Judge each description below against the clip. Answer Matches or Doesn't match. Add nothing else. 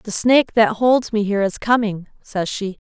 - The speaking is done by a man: Doesn't match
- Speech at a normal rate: Doesn't match